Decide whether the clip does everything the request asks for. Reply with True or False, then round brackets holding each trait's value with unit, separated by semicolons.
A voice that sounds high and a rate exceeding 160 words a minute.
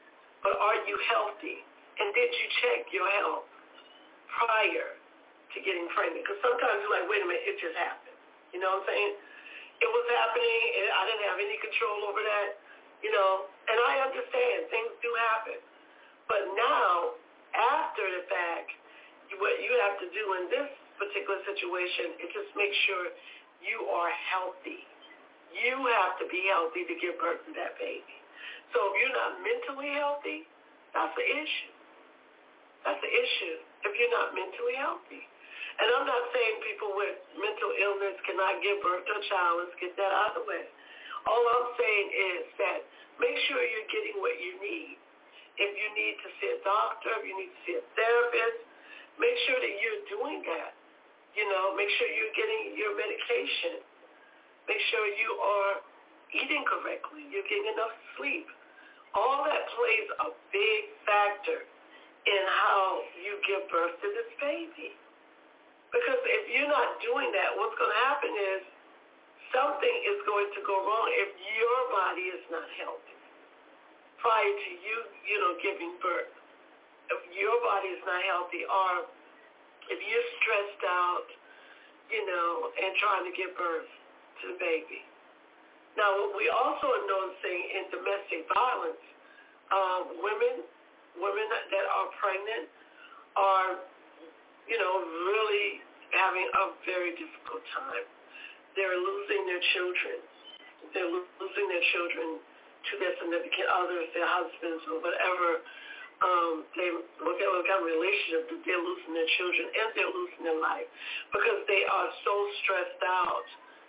False (270 Hz; 155 wpm)